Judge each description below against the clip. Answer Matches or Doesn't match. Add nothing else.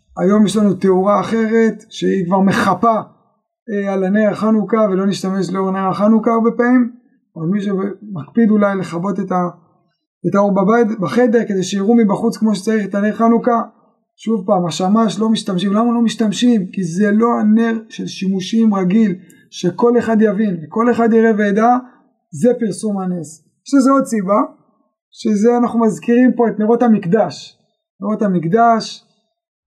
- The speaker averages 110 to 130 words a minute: Doesn't match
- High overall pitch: Matches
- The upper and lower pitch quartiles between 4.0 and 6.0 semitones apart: Doesn't match